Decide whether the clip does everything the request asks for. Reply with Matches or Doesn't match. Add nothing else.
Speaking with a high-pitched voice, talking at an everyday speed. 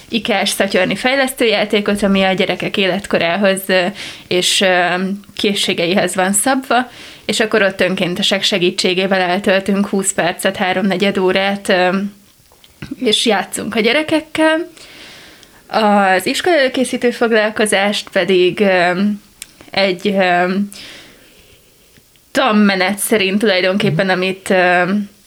Doesn't match